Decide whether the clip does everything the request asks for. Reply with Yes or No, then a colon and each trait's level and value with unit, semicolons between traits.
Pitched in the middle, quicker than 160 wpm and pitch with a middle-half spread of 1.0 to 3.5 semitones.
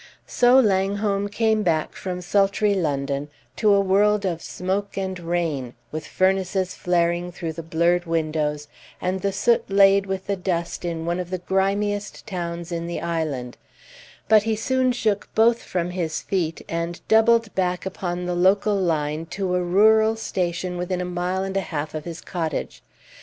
Yes: medium, 180 Hz; average, 170 wpm; average, 2.9 semitones